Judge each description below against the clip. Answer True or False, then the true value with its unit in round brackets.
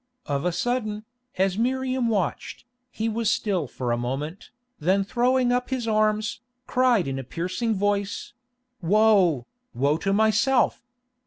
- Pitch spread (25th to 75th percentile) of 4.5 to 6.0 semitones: True (5.1 semitones)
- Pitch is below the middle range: False (210 Hz)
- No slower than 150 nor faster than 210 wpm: False (140 wpm)